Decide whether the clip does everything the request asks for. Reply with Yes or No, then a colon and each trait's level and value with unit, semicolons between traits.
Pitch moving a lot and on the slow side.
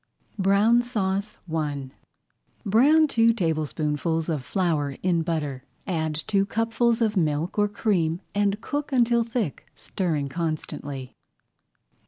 Yes: wide, 6.2 semitones; slow, 115 wpm